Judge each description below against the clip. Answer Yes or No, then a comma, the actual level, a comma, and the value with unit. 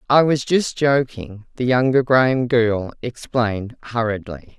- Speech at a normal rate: No, slow, 130 wpm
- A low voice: Yes, low, 120 Hz